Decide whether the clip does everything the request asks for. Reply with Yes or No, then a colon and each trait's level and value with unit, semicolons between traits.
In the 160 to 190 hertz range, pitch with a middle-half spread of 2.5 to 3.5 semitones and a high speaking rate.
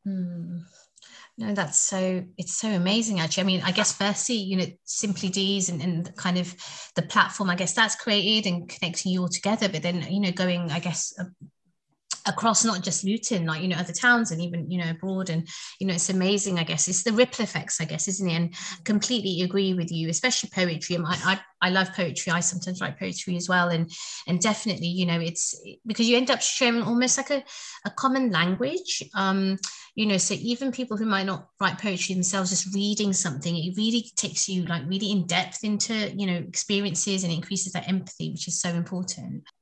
Yes: medium, 185 Hz; average, 2.8 semitones; fast, 210 wpm